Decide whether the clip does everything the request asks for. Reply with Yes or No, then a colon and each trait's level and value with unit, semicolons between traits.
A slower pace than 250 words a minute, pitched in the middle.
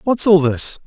Yes: fast, 210 wpm; medium, 175 Hz